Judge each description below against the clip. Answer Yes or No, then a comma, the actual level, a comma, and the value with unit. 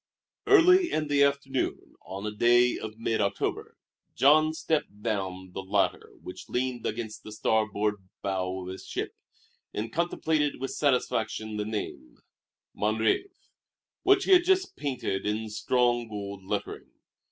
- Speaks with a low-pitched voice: Yes, low, 110 Hz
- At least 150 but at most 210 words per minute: No, average, 140 wpm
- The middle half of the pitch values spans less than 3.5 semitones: No, wide, 5.6 semitones